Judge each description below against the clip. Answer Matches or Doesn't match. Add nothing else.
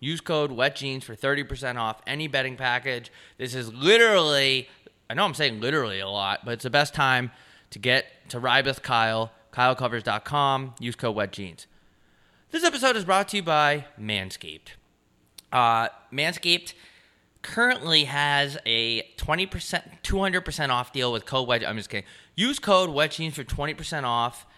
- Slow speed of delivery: Doesn't match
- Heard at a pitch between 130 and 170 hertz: Matches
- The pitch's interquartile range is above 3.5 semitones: Matches